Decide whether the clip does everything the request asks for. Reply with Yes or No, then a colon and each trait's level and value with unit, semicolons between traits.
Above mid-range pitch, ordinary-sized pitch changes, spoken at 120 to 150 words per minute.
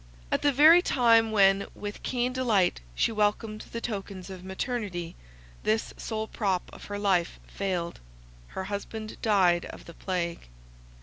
Yes: high, 205 Hz; average, 3.2 semitones; average, 145 wpm